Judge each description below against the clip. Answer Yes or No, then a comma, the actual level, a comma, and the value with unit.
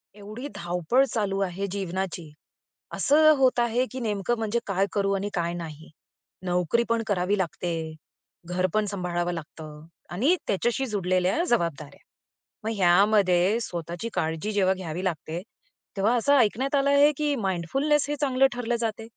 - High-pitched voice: Yes, high, 195 Hz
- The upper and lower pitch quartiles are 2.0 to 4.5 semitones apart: No, average, 5.2 semitones